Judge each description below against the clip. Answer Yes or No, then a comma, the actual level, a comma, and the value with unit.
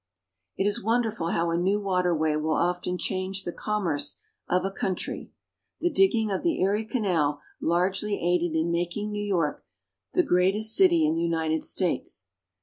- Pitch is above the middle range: No, medium, 180 Hz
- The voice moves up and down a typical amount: Yes, average, 3.6 semitones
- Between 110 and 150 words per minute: No, average, 165 wpm